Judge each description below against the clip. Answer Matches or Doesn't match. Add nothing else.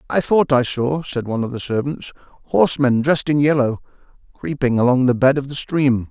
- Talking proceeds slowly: Doesn't match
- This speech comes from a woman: Doesn't match